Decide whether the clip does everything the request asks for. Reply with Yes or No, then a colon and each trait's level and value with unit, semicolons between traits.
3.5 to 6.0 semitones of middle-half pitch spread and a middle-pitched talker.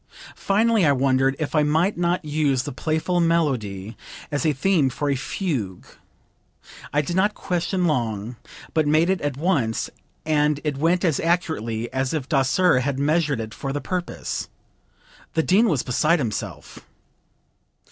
Yes: average, 4.5 semitones; medium, 150 Hz